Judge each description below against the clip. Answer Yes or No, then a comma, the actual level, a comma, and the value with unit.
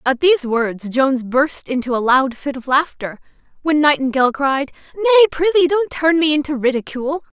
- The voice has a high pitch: Yes, very high, 285 Hz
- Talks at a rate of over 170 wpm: No, average, 160 wpm